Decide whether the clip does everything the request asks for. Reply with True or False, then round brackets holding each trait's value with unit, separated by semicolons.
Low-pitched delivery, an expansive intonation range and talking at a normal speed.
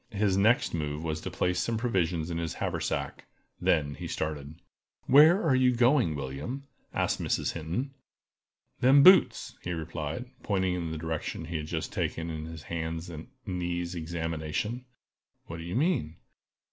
True (85 Hz; 6.0 semitones; 160 wpm)